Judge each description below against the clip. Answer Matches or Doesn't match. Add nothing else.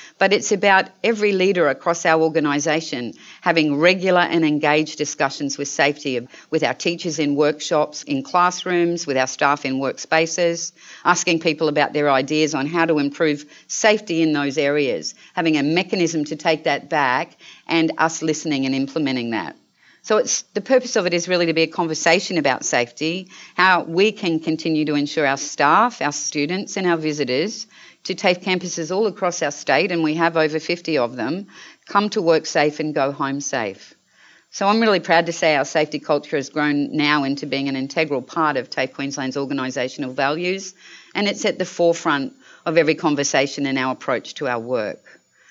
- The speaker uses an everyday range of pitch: Matches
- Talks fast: Doesn't match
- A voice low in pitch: Doesn't match